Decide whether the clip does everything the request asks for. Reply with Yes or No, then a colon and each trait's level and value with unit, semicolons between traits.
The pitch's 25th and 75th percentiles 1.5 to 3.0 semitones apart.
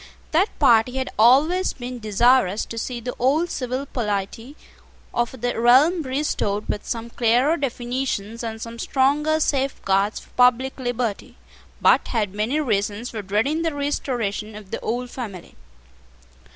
No: average, 3.5 semitones